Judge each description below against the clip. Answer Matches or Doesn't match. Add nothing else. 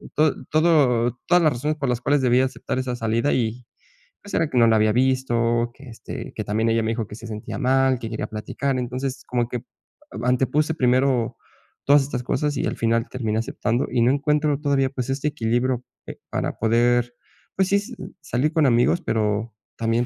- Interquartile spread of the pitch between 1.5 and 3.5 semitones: Matches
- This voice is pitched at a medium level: Doesn't match